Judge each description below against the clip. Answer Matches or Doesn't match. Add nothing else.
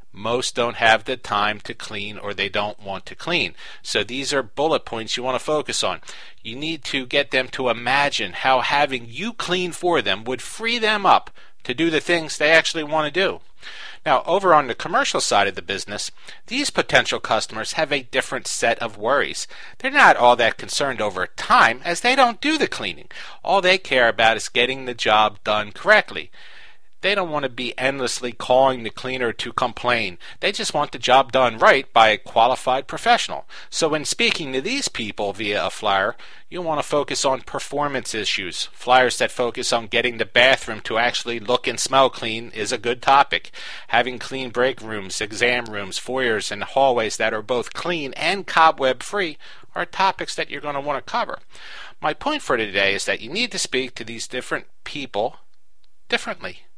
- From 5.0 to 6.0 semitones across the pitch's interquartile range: Matches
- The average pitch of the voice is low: Matches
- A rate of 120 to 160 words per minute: Doesn't match